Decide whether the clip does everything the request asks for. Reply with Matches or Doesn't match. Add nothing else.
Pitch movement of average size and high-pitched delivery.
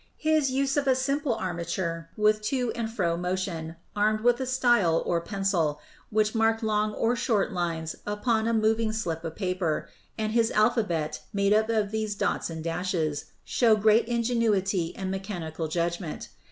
Matches